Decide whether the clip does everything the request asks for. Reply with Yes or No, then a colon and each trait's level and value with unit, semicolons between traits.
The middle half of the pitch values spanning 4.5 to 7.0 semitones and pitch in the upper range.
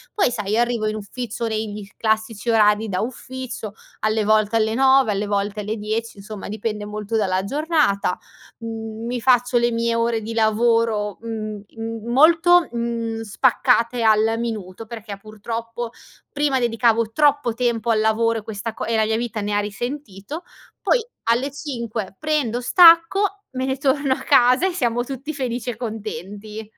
No: narrow, 2.4 semitones; high, 230 Hz